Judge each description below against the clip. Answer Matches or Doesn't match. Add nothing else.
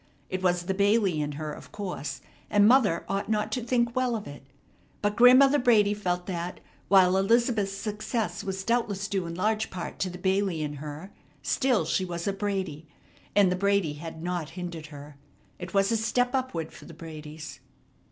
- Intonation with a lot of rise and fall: Doesn't match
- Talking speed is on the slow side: Doesn't match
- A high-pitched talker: Matches